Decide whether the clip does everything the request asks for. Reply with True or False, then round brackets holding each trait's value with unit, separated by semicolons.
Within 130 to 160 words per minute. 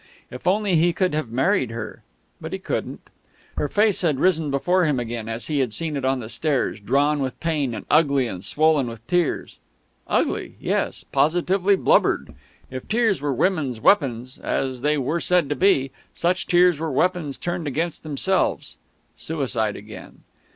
False (170 wpm)